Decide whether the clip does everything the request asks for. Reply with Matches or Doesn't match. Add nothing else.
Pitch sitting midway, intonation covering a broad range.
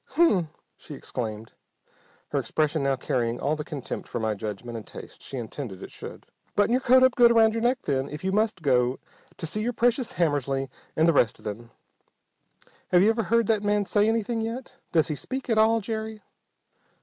Matches